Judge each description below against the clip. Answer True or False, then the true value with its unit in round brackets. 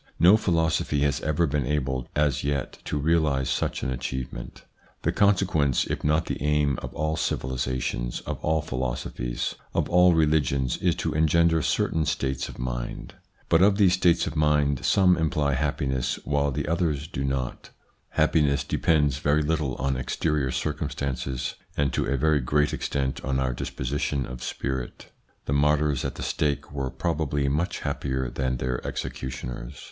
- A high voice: False (70 Hz)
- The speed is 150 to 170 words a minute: True (160 wpm)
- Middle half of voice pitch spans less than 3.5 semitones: True (3.1 semitones)